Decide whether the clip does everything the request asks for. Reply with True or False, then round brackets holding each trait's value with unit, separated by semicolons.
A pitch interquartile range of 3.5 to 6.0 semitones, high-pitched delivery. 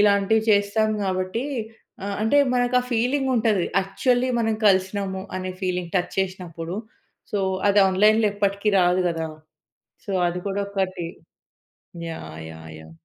False (2.9 semitones; 195 Hz)